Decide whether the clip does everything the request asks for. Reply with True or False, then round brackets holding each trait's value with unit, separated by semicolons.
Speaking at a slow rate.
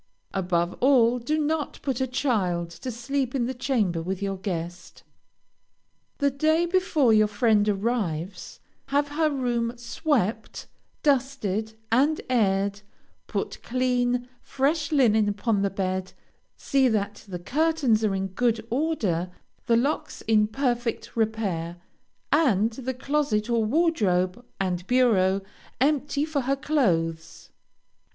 True (125 wpm)